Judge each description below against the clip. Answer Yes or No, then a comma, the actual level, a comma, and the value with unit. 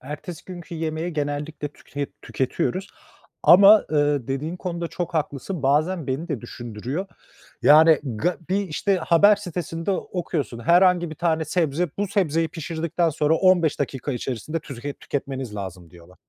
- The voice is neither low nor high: Yes, medium, 160 Hz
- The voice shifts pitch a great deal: No, average, 3.9 semitones